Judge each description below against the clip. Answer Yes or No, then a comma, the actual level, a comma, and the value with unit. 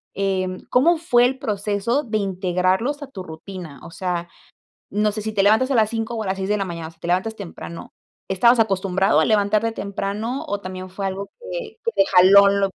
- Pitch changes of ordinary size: Yes, average, 3.3 semitones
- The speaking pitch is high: Yes, high, 200 Hz